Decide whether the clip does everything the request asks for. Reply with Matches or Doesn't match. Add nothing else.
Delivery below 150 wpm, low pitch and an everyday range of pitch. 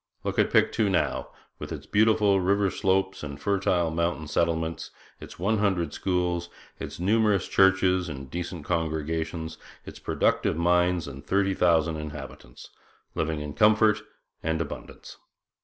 Matches